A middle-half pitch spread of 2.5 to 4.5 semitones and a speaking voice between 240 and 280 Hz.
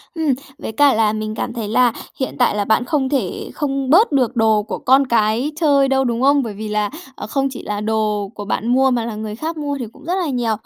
Yes: average, 4.2 semitones; high, 245 Hz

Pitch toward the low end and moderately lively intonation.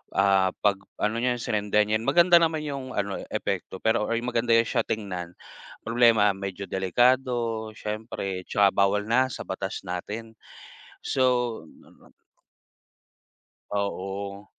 Yes: low, 105 Hz; average, 3.3 semitones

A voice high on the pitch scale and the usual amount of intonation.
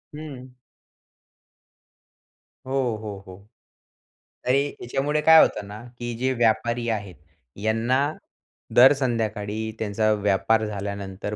No: low, 110 Hz; average, 3.6 semitones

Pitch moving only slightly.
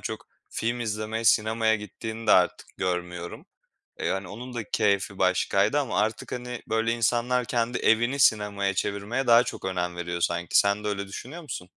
No: average, 3.2 semitones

